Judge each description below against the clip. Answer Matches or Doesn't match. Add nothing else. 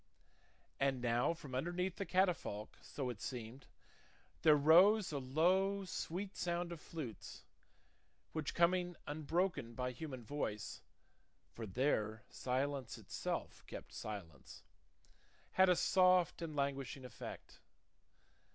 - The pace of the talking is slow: Matches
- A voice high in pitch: Doesn't match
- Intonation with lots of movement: Matches